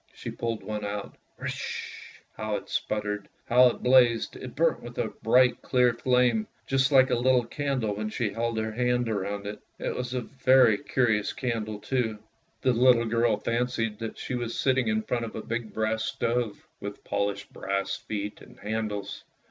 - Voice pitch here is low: Yes, low, 115 Hz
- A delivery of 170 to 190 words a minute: Yes, average, 180 wpm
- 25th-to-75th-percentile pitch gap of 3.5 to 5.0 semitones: No, average, 2.8 semitones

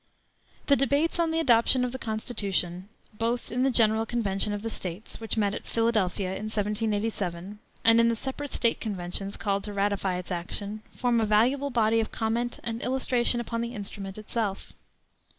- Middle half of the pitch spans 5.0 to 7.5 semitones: No, average, 3.0 semitones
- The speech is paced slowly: No, average, 175 wpm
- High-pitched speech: Yes, high, 220 Hz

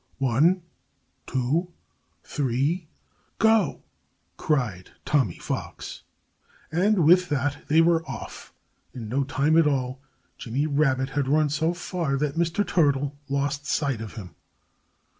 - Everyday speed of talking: No, slow, 120 wpm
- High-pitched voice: No, medium, 145 Hz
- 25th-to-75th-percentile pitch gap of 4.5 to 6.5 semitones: No, average, 3.7 semitones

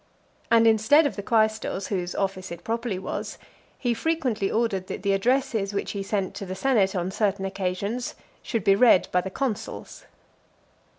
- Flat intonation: No, average, 3.2 semitones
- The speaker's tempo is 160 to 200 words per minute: Yes, average, 170 wpm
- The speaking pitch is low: No, high, 205 Hz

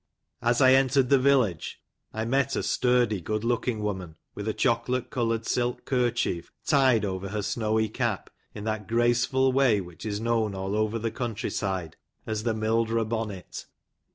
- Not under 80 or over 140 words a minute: No, average, 170 wpm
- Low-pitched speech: Yes, low, 115 Hz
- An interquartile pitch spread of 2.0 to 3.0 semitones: Yes, average, 2.7 semitones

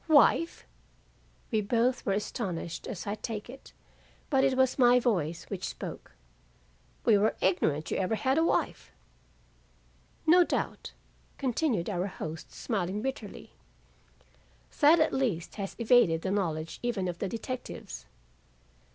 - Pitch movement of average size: No, wide, 6.0 semitones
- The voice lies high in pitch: Yes, high, 215 Hz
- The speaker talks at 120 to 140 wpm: Yes, slow, 135 wpm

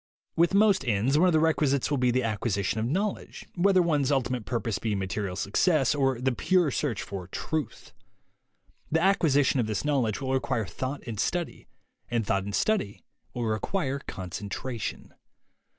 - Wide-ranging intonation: Yes, wide, 6.4 semitones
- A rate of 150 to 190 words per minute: Yes, average, 170 wpm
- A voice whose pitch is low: Yes, low, 130 Hz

